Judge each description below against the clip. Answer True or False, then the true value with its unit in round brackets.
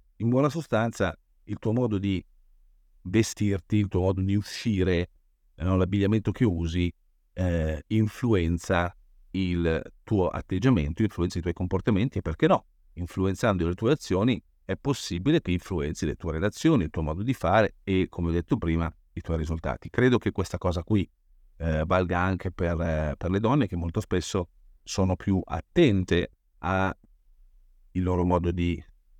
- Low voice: True (90 Hz)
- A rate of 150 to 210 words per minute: True (155 wpm)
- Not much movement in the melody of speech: False (3.4 semitones)